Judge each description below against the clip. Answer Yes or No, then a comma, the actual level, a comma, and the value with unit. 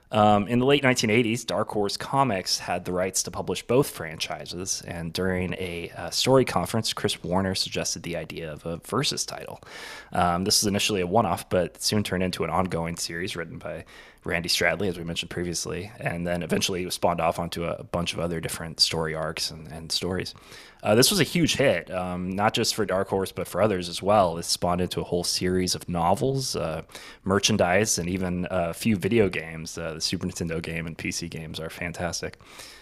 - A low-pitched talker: Yes, very low, 90 Hz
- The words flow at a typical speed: No, fast, 210 wpm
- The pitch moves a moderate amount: Yes, average, 3.6 semitones